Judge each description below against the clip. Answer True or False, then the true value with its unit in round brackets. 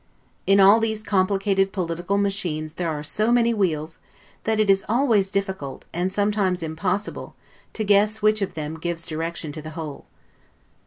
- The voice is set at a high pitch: True (195 Hz)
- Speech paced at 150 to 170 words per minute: True (165 wpm)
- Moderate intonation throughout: True (4.1 semitones)